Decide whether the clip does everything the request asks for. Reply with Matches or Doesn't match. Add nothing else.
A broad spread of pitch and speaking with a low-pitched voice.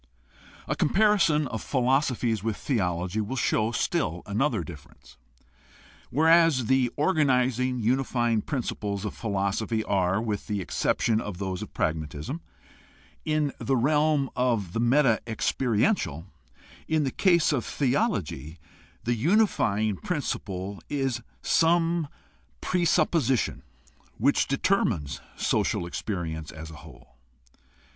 Matches